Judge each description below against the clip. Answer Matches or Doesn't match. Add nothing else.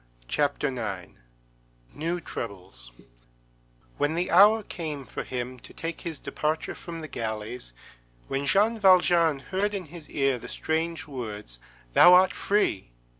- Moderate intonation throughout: Doesn't match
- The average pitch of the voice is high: Doesn't match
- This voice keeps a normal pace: Doesn't match